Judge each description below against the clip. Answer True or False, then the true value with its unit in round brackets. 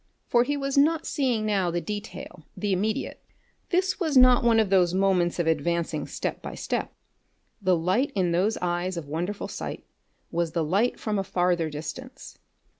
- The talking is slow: False (175 wpm)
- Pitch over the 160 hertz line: True (190 Hz)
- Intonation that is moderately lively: False (5.7 semitones)